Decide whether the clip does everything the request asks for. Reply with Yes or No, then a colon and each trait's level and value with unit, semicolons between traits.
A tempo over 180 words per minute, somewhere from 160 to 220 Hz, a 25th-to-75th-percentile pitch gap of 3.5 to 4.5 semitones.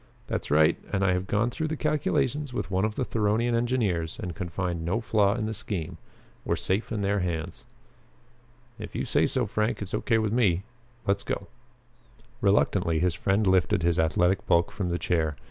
No: average, 190 wpm; low, 100 Hz; average, 4.1 semitones